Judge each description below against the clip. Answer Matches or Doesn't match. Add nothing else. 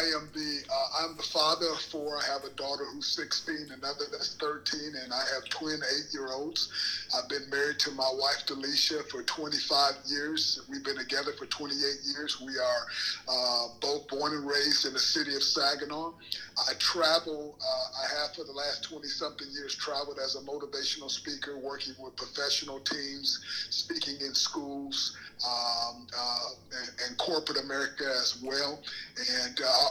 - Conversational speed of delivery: Matches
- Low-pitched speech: Doesn't match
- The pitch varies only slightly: Matches